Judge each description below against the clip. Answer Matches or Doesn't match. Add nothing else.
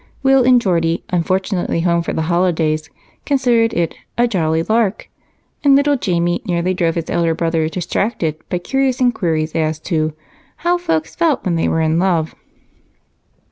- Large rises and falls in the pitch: Matches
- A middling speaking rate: Matches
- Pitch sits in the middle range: Matches